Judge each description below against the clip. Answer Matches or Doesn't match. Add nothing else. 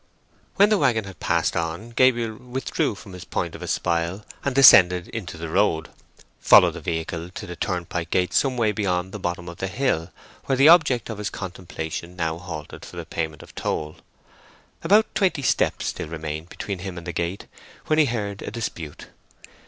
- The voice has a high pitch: Doesn't match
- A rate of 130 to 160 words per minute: Doesn't match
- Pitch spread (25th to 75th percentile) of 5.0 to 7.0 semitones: Matches